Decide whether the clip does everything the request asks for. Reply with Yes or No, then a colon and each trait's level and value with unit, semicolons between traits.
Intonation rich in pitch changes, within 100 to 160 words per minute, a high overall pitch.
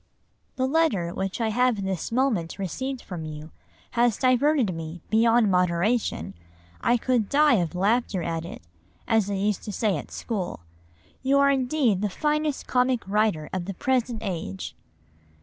Yes: wide, 5.8 semitones; average, 155 wpm; high, 215 Hz